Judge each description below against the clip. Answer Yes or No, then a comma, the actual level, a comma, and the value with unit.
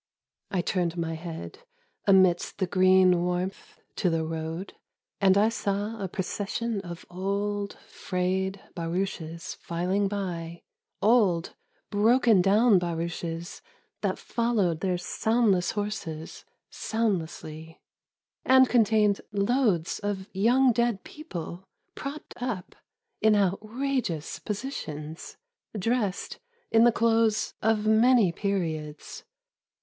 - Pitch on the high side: Yes, high, 195 Hz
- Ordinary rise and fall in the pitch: Yes, average, 4.1 semitones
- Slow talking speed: Yes, slow, 105 wpm